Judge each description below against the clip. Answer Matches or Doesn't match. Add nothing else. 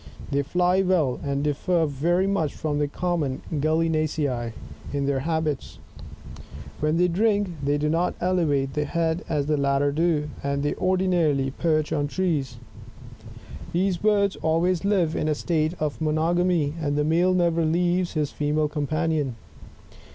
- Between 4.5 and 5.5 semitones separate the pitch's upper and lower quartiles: Doesn't match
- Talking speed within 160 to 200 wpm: Doesn't match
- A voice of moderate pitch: Matches